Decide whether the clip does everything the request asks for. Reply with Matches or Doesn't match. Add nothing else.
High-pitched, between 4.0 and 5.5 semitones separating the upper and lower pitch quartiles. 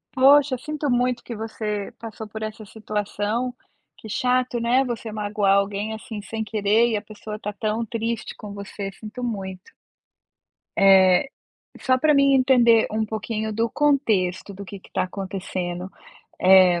Doesn't match